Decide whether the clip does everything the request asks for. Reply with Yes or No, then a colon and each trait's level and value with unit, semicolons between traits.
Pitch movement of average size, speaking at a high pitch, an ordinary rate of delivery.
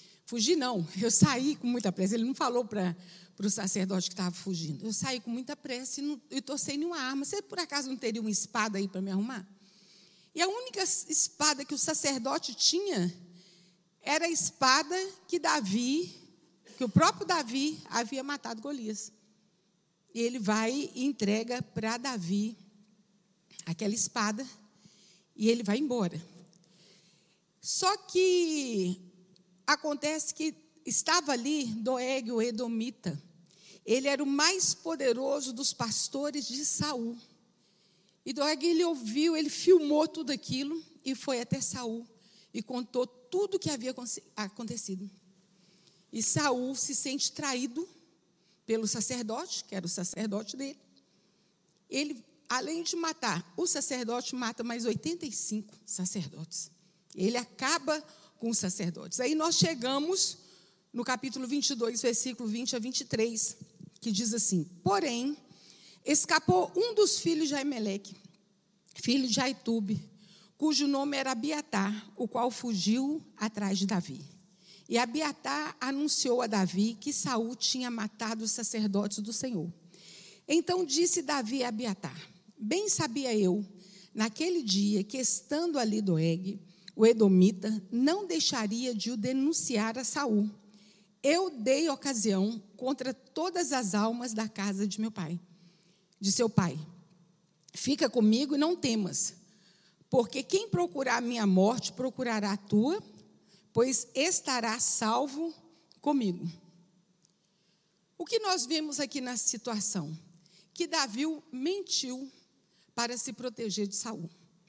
No: wide, 6.3 semitones; high, 230 Hz; average, 130 wpm